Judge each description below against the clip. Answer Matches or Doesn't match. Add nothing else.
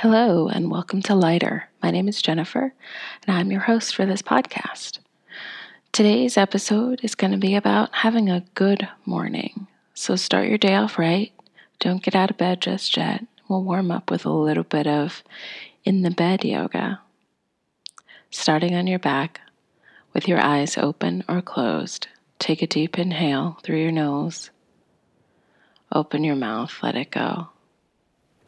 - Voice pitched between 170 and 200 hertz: Matches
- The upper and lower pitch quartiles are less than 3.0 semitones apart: Doesn't match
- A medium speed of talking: Matches